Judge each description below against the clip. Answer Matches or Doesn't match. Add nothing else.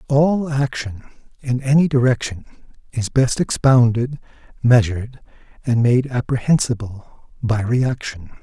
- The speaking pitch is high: Doesn't match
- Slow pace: Matches